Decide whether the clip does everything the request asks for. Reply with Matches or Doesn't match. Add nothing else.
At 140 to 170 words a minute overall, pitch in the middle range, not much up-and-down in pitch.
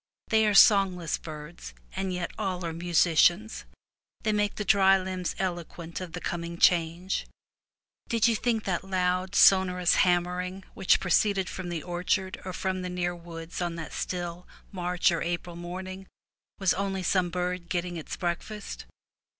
Matches